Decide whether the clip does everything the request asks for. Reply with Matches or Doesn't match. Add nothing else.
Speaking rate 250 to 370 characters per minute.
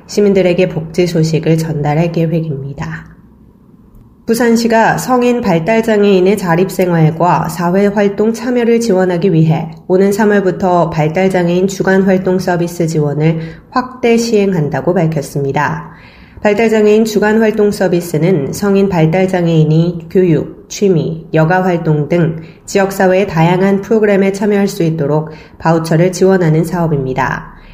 Matches